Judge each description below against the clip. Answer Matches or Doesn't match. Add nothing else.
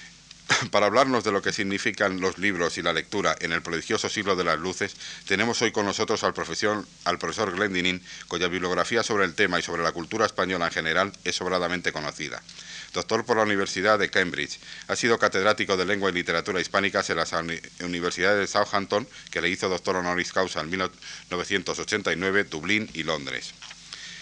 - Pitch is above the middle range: Doesn't match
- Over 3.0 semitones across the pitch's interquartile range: Doesn't match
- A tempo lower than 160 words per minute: Doesn't match